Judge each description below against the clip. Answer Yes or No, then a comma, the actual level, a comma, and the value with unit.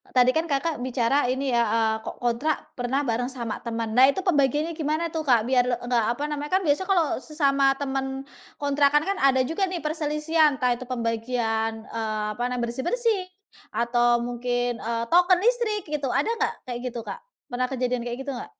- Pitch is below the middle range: No, very high, 265 Hz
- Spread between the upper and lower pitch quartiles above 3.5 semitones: Yes, average, 4.0 semitones